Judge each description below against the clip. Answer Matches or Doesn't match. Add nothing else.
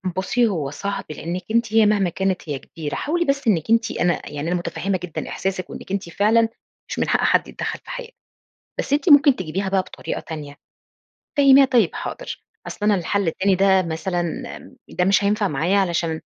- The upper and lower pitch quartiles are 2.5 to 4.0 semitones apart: Doesn't match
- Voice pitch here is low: Doesn't match